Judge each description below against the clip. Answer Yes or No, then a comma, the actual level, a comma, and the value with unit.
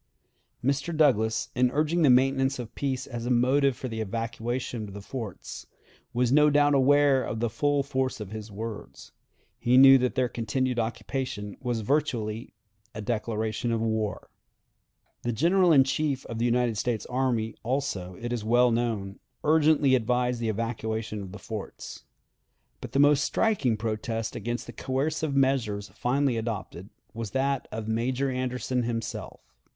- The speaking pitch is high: No, low, 120 Hz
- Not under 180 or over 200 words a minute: No, average, 155 wpm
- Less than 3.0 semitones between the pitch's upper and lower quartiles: No, average, 3.3 semitones